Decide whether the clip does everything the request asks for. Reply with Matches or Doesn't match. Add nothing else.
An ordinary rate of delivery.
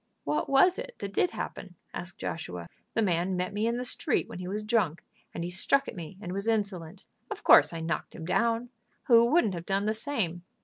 Doesn't match